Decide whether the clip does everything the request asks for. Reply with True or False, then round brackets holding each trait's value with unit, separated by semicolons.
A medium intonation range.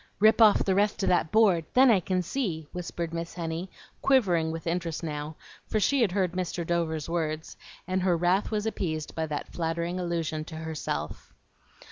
True (3.0 semitones)